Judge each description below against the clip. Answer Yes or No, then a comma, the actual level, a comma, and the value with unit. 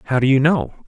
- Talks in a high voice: No, low, 135 Hz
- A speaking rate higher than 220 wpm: Yes, fast, 275 wpm